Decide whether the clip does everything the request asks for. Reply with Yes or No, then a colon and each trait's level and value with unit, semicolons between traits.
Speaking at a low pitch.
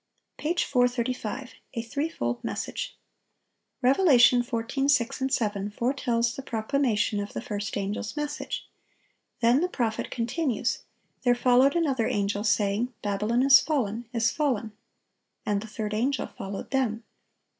No: high, 240 Hz